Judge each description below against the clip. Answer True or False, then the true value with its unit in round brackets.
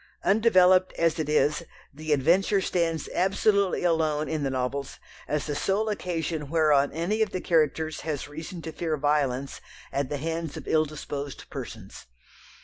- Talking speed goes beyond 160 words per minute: False (155 wpm)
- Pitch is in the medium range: True (160 Hz)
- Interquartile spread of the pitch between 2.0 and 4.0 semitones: True (3.4 semitones)